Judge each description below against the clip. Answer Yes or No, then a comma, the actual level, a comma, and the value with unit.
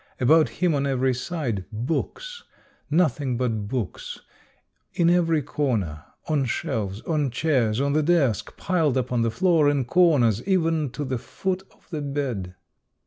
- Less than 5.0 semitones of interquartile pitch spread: No, average, 5.3 semitones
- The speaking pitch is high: No, medium, 140 Hz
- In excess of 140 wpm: Yes, average, 155 wpm